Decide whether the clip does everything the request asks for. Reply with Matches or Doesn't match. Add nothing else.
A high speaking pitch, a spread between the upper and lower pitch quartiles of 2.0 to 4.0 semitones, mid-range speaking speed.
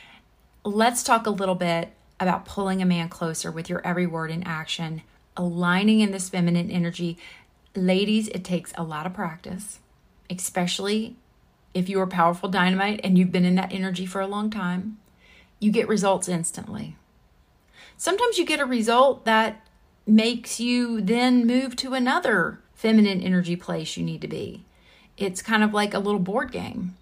Matches